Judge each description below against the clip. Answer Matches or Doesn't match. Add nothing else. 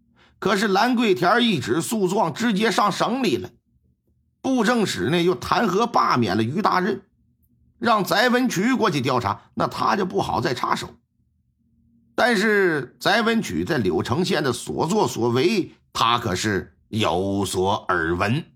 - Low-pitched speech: Doesn't match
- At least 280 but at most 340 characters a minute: Doesn't match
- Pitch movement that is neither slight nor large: Doesn't match